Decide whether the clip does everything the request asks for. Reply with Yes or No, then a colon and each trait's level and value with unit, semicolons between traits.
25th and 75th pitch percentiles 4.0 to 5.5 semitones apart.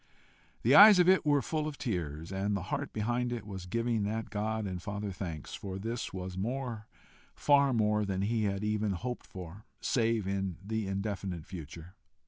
No: average, 3.6 semitones